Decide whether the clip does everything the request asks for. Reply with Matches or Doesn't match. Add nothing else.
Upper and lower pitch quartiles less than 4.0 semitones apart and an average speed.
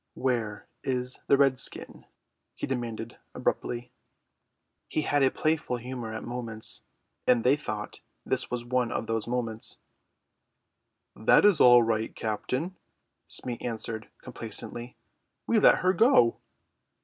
Doesn't match